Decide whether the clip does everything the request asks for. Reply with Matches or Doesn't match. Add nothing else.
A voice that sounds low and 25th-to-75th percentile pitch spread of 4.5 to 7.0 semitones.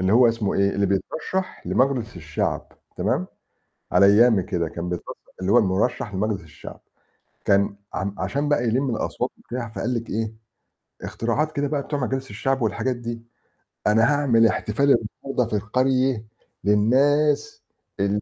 Matches